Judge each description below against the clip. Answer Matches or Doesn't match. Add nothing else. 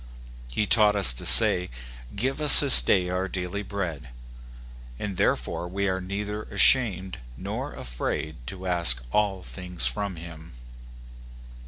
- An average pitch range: Matches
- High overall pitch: Doesn't match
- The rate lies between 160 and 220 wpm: Doesn't match